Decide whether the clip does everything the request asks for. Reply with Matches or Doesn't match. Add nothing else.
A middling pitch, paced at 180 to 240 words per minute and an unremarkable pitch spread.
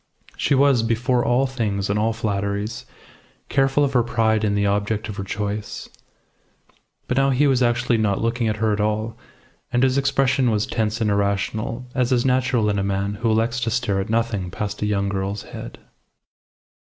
Doesn't match